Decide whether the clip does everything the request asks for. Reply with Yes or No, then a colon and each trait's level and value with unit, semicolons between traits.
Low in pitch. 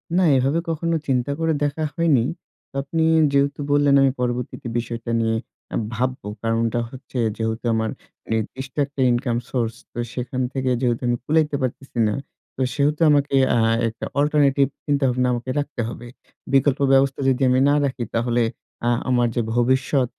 Yes: low, 130 Hz